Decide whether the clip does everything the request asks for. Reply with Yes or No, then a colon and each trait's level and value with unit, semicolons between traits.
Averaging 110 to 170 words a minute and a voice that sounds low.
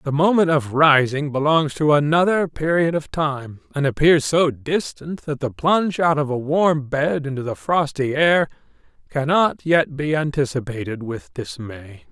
No: average, 160 wpm; medium, 145 Hz